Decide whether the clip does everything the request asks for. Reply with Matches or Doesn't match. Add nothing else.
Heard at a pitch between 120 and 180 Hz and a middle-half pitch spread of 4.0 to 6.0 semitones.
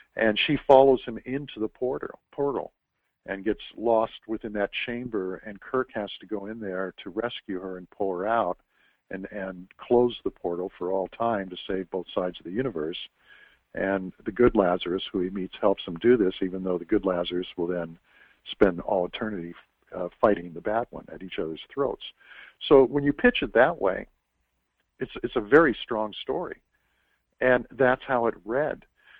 Doesn't match